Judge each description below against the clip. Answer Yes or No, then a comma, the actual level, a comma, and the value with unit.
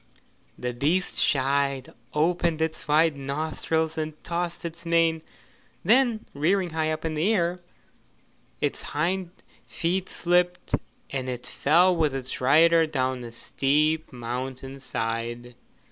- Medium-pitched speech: Yes, medium, 155 Hz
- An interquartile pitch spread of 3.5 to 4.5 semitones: Yes, average, 4.0 semitones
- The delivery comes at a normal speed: No, slow, 125 wpm